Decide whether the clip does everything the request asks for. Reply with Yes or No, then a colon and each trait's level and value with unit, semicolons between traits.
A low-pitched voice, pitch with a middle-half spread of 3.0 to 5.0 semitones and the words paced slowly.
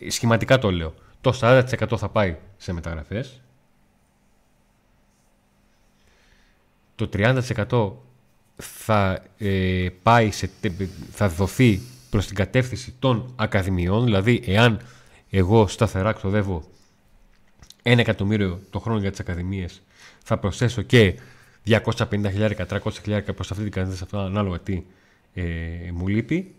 Yes: low, 105 Hz; average, 3.3 semitones; slow, 110 wpm